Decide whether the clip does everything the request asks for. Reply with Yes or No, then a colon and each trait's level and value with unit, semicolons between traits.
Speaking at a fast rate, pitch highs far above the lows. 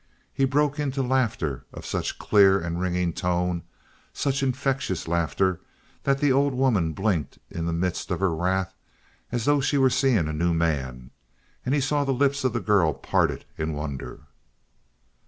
No: average, 170 wpm; wide, 8.2 semitones